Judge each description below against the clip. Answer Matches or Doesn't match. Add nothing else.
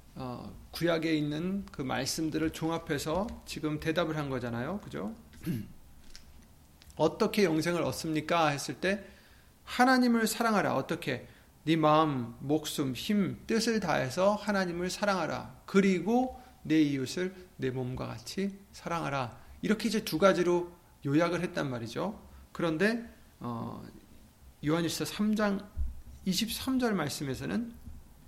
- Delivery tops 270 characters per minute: Doesn't match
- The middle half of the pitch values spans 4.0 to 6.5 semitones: Matches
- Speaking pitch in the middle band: Matches